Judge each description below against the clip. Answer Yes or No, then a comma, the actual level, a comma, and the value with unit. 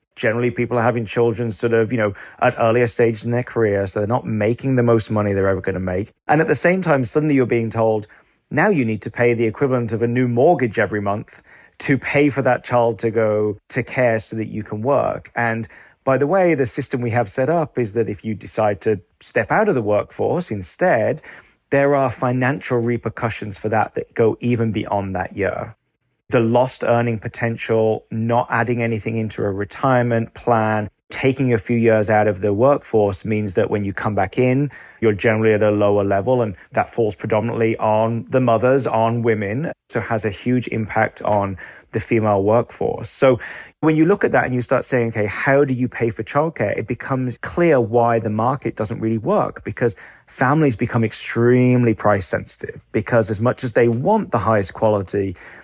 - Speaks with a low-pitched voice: Yes, low, 115 Hz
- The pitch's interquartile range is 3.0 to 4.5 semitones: No, narrow, 2.6 semitones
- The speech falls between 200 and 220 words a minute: Yes, fast, 205 wpm